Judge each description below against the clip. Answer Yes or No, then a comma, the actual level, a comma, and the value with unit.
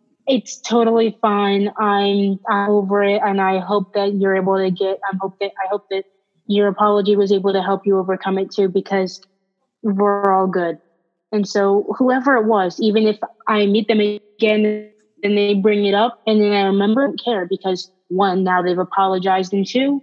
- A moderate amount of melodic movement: No, narrow, 1.7 semitones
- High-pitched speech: Yes, high, 200 Hz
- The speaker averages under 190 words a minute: No, average, 195 wpm